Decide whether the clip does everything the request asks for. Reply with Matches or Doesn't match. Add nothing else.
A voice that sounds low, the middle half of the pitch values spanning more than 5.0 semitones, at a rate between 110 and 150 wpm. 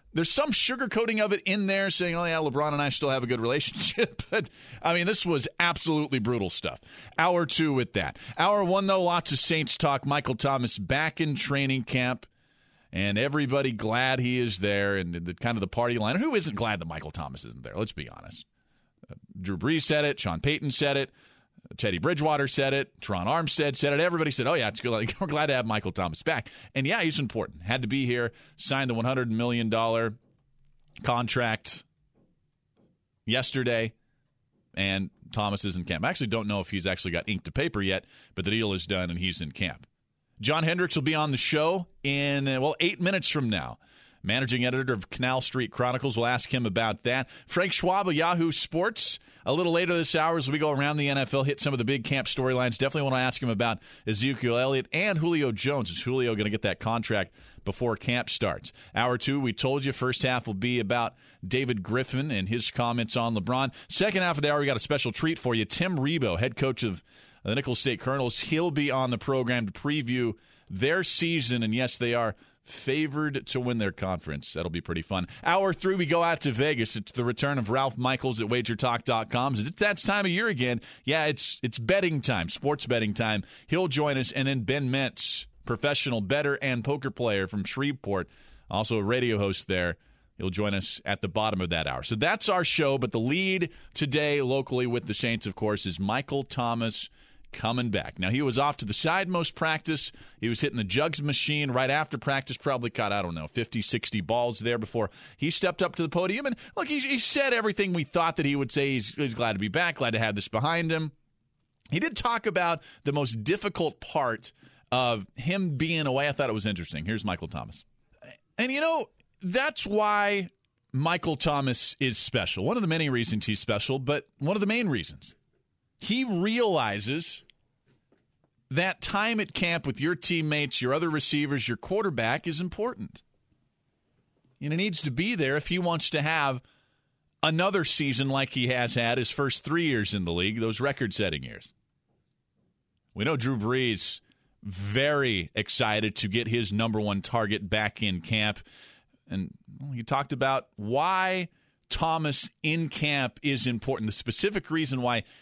Doesn't match